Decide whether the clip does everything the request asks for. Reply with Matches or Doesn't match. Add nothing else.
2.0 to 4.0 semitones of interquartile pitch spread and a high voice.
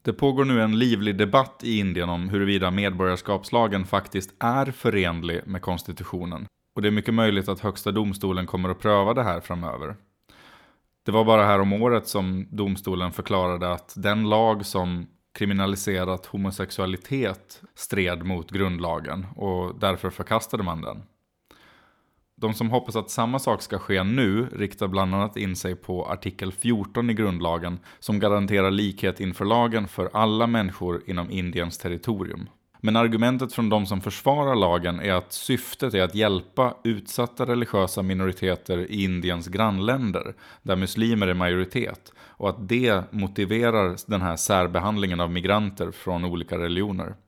Doesn't match